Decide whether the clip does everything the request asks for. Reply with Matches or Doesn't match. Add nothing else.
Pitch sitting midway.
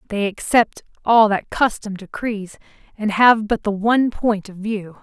Doesn't match